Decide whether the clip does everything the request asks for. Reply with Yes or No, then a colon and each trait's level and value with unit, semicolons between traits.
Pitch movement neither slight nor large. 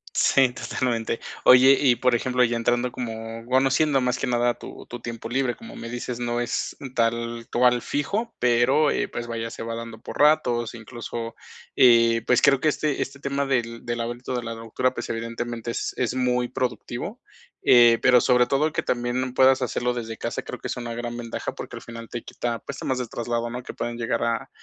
No: narrow, 1.6 semitones